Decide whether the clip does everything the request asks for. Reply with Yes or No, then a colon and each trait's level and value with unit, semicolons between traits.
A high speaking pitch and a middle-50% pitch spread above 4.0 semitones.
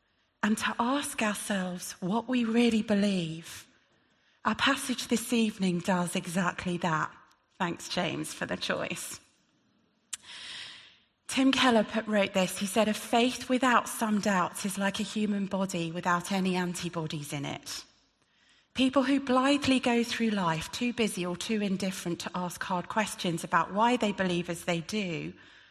Yes: high, 205 Hz; average, 4.6 semitones